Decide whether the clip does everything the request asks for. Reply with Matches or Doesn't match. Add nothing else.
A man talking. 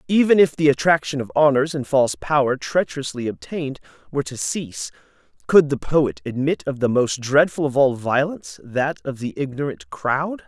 Matches